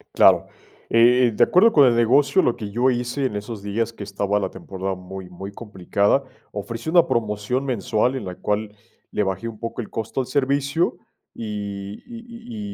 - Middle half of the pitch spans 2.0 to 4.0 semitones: No, average, 4.5 semitones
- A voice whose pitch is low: Yes, low, 115 Hz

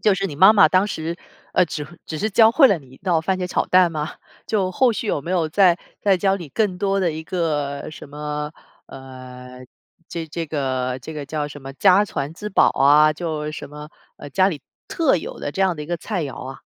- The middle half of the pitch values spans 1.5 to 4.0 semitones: No, average, 4.5 semitones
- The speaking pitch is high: No, medium, 160 Hz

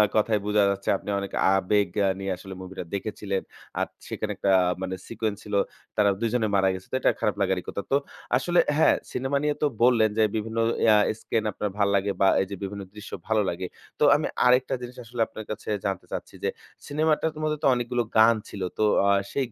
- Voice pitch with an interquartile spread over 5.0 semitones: No, average, 3.6 semitones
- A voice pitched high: No, low, 105 Hz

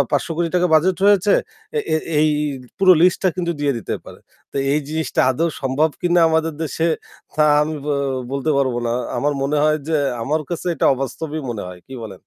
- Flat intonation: No, average, 3.6 semitones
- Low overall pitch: No, medium, 155 Hz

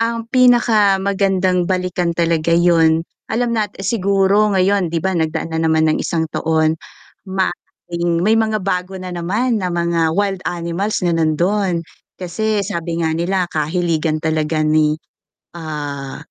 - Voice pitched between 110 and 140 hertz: No, medium, 175 Hz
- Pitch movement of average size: Yes, average, 3.4 semitones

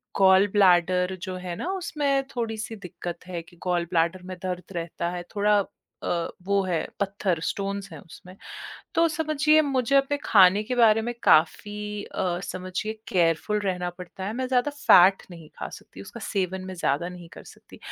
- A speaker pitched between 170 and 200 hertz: Yes, high, 190 Hz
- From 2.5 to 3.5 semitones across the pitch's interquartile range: No, average, 3.9 semitones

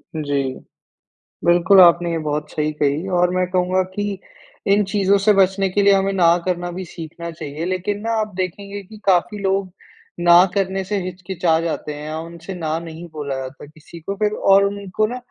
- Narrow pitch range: No, average, 3.0 semitones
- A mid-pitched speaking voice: Yes, medium, 180 Hz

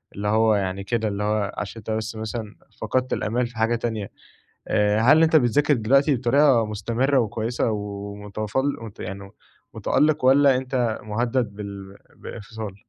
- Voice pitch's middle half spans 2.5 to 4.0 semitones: Yes, average, 3.4 semitones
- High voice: No, low, 110 Hz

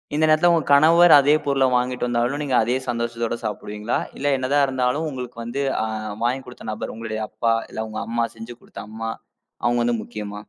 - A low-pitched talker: Yes, low, 125 Hz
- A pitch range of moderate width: Yes, average, 3.3 semitones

